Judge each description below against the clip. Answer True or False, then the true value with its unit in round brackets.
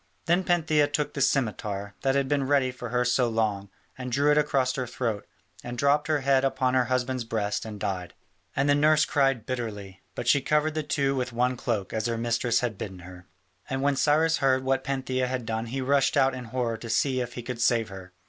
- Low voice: True (130 Hz)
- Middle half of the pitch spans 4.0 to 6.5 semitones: False (3.3 semitones)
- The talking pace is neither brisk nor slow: False (225 wpm)